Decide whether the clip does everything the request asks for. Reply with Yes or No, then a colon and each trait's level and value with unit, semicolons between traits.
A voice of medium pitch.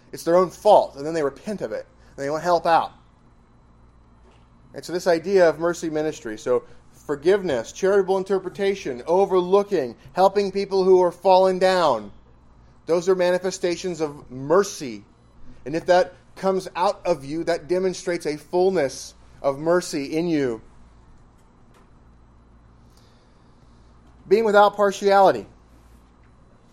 Yes: medium, 165 Hz